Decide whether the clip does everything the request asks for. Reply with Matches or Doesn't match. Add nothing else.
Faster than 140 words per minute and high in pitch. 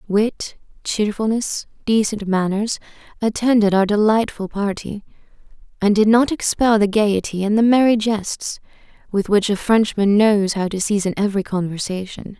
Doesn't match